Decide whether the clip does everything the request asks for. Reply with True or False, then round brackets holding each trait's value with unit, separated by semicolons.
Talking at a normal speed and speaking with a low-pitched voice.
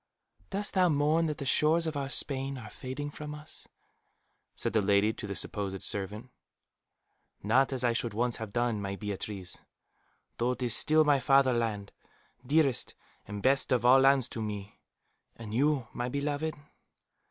True (165 wpm; 125 Hz)